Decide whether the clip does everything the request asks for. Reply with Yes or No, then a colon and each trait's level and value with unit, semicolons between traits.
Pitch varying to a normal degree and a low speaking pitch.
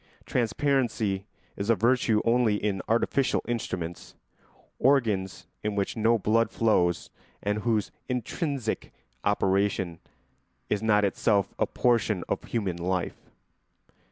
Yes: average, 3.1 semitones; low, 105 Hz